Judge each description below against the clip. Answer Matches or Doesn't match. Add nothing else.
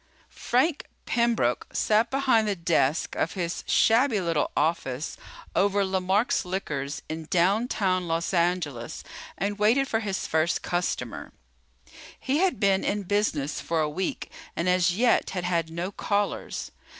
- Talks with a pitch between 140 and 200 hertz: Matches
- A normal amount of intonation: Matches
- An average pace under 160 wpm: Matches